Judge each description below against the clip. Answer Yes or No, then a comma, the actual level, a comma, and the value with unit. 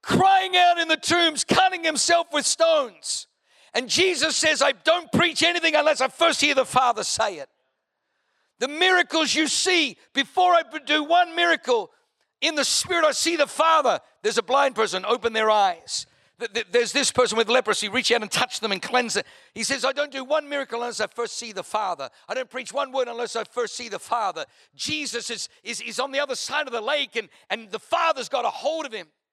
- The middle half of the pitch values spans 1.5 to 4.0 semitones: No, average, 5.3 semitones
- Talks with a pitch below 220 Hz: No, very high, 280 Hz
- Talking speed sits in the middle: No, fast, 215 wpm